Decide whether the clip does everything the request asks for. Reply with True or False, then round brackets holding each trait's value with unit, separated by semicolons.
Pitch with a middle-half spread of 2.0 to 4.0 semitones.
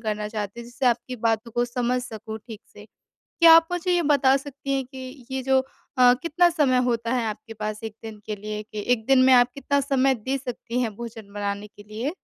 True (3.6 semitones)